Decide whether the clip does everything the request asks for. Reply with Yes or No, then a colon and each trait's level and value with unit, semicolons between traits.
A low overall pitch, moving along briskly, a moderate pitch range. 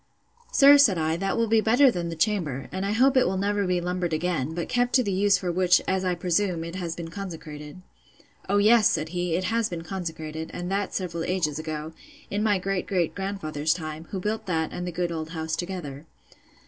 No: medium, 180 Hz; fast, 220 wpm; average, 3.7 semitones